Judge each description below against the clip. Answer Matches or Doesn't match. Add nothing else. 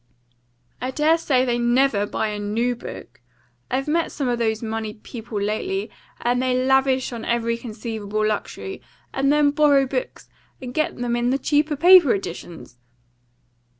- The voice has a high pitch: Matches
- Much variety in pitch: Doesn't match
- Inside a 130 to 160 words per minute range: Matches